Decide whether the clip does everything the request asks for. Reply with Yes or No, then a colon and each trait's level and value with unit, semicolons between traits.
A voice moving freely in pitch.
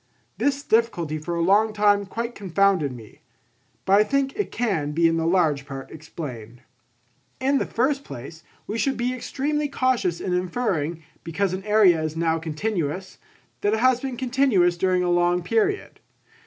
Yes: wide, 6.7 semitones